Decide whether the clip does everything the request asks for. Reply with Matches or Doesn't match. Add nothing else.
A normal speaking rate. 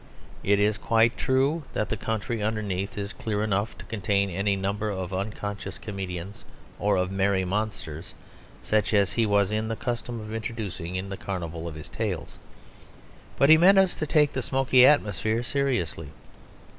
Matches